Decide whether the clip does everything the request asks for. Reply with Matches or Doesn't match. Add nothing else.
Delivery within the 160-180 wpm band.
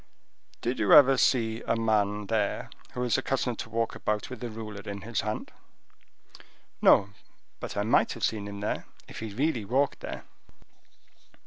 Matches